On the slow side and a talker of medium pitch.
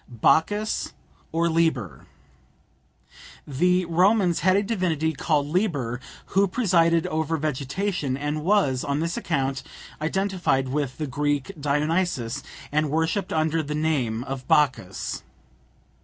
Yes: slow, 115 wpm; medium, 155 Hz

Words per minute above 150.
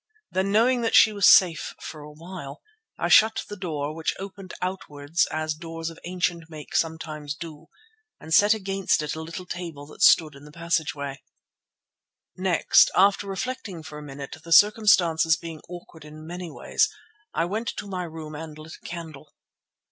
Yes: average, 170 wpm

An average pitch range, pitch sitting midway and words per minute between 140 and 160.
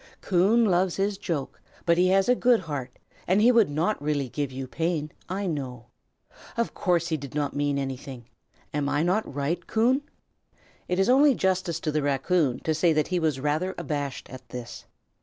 No: average, 4.8 semitones; medium, 160 Hz; average, 190 wpm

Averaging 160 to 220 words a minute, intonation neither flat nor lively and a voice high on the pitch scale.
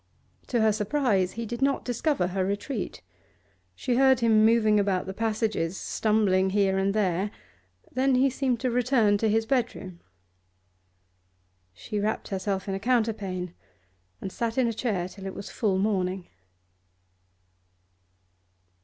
No: average, 140 wpm; average, 3.7 semitones; high, 215 Hz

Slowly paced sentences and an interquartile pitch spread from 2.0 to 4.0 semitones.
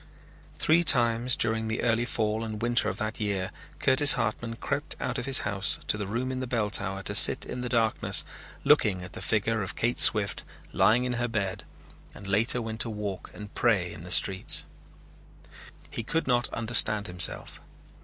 No: average, 185 wpm; average, 2.8 semitones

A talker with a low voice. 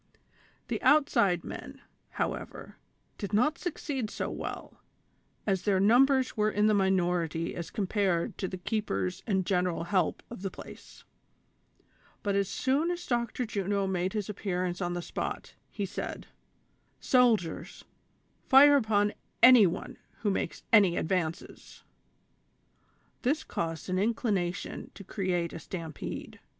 No: high, 200 Hz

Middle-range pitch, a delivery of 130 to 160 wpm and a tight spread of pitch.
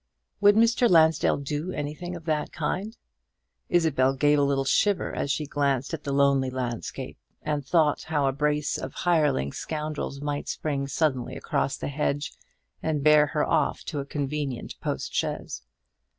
Yes: medium, 150 Hz; average, 155 wpm; narrow, 2.3 semitones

